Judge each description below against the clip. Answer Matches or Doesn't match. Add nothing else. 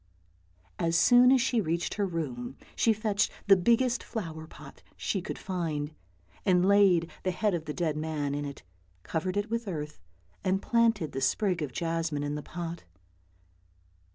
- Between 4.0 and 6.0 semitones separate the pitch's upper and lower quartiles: Matches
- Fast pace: Doesn't match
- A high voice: Doesn't match